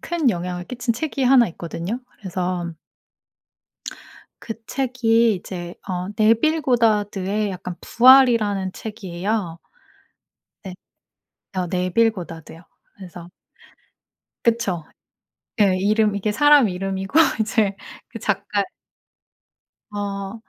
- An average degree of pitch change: Yes, average, 4.0 semitones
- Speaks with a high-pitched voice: Yes, high, 205 Hz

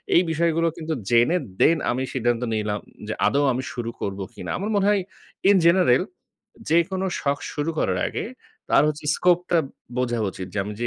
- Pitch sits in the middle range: Yes, medium, 145 Hz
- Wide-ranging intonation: Yes, wide, 6.0 semitones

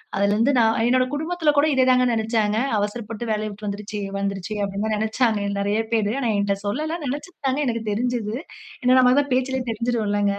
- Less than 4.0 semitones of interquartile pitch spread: Yes, average, 3.6 semitones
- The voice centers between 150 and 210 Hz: No, high, 225 Hz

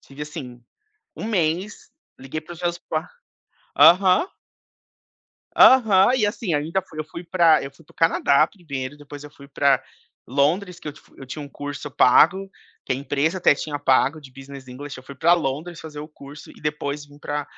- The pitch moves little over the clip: No, average, 3.7 semitones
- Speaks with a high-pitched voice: No, medium, 150 Hz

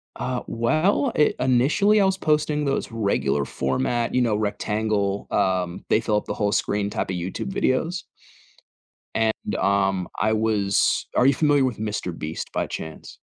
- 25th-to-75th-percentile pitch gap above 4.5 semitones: Yes, wide, 5.5 semitones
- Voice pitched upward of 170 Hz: No, low, 110 Hz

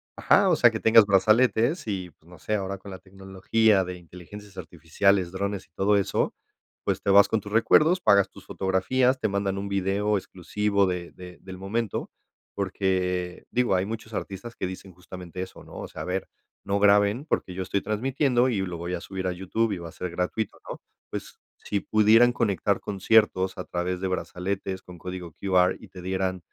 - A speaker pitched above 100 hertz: No, very low, 95 Hz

